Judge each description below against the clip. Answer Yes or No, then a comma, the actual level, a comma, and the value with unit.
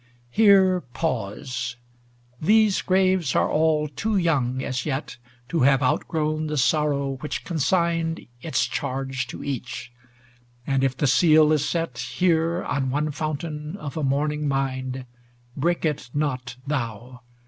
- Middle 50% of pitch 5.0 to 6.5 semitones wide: No, average, 3.7 semitones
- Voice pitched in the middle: Yes, medium, 150 Hz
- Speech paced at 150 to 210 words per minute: No, average, 140 wpm